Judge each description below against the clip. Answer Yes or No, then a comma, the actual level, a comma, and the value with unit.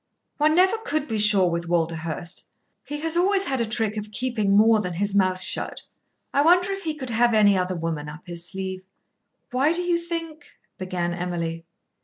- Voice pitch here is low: No, high, 210 Hz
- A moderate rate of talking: Yes, average, 195 wpm